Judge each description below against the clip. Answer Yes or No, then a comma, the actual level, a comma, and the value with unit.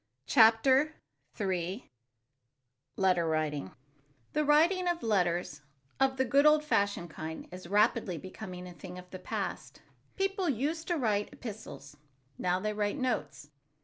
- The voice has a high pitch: Yes, high, 210 Hz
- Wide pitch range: Yes, wide, 7.5 semitones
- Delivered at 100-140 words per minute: Yes, slow, 135 wpm